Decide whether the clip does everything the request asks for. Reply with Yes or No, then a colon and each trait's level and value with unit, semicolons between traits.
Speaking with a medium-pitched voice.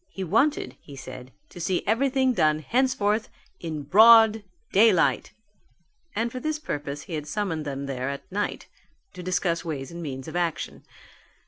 Yes: medium, 175 Hz